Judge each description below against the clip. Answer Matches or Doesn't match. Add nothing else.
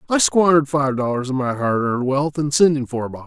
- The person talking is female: Doesn't match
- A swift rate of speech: Matches